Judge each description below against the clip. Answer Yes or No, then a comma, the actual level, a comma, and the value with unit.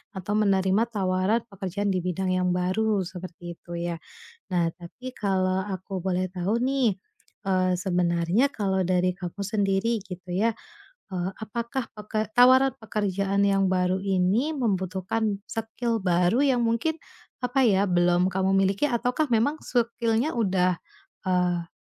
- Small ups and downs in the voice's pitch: No, average, 3.6 semitones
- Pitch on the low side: No, high, 195 Hz